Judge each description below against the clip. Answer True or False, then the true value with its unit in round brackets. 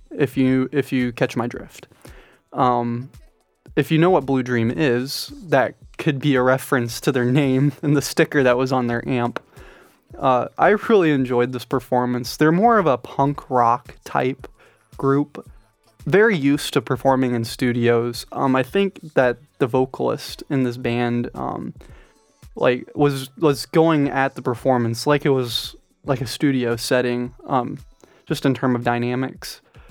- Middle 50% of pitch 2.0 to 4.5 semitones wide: True (2.7 semitones)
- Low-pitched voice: True (130 Hz)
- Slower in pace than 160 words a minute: False (165 wpm)